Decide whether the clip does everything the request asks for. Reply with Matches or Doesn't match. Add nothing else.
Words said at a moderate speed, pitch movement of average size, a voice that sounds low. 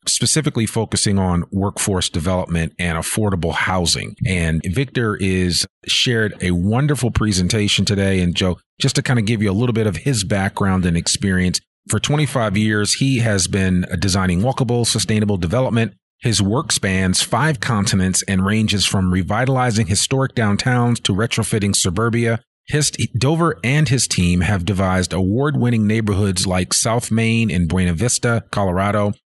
Matches